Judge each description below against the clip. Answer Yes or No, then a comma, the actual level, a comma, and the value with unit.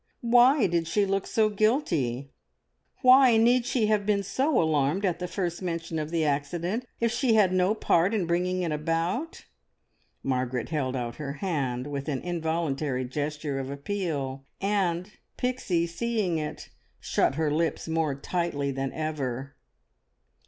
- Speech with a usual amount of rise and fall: No, wide, 5.9 semitones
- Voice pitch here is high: No, medium, 170 Hz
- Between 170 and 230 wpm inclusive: No, average, 150 wpm